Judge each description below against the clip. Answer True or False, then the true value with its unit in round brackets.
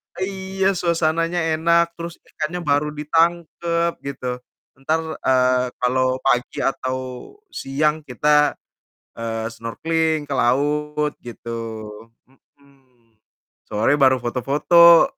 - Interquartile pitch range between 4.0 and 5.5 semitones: True (4.5 semitones)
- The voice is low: False (150 Hz)